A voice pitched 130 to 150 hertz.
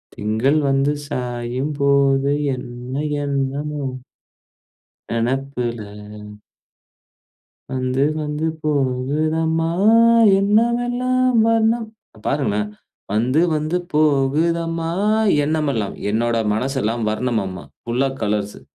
Yes: low, 135 Hz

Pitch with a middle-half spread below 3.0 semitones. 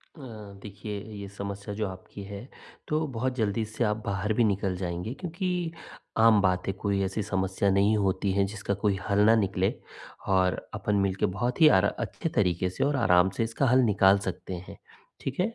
Yes: narrow, 2.6 semitones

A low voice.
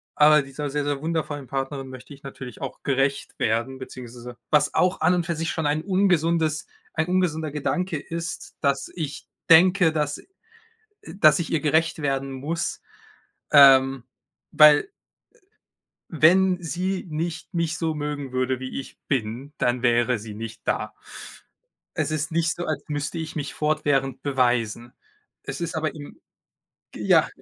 No: medium, 150 Hz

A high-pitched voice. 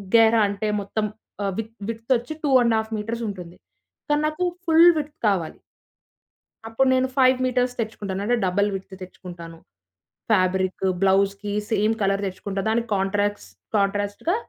Yes: high, 210 Hz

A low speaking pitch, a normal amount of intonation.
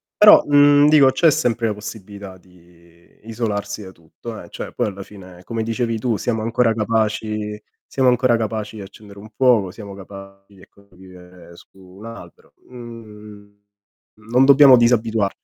Yes: low, 105 Hz; average, 3.2 semitones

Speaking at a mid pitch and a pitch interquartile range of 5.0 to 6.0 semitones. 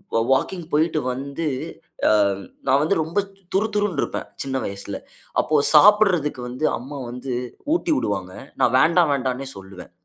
Yes: medium, 145 Hz; average, 5.3 semitones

